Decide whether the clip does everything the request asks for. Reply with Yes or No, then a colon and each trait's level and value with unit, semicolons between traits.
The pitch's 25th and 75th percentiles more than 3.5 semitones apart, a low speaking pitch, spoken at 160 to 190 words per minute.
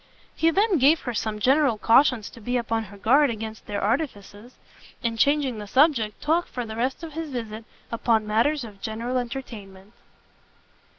No: average, 4.3 semitones; high, 235 Hz; average, 170 wpm